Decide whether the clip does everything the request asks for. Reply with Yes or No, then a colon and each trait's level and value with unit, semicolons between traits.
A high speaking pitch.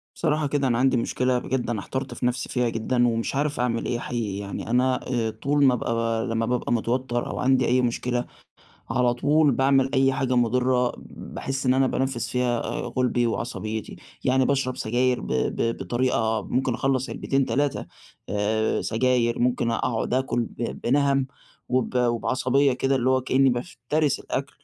No: low, 125 Hz